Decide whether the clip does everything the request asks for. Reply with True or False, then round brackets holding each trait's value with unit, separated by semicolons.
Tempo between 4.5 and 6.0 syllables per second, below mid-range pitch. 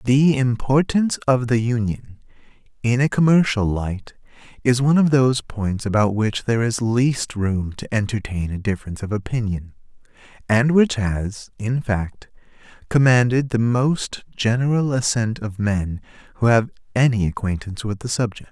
True (4.7 syllables/s; 115 Hz)